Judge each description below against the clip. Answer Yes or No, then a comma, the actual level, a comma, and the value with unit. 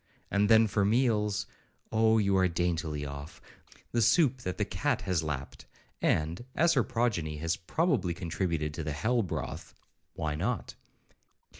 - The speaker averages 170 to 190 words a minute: No, average, 140 wpm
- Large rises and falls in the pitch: Yes, wide, 5.9 semitones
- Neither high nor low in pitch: No, very low, 95 Hz